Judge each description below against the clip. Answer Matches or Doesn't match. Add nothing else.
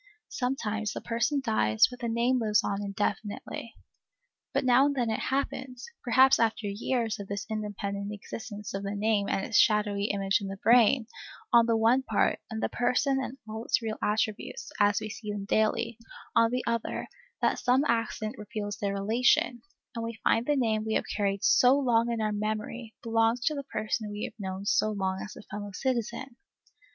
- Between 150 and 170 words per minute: Doesn't match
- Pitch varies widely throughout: Doesn't match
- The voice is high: Matches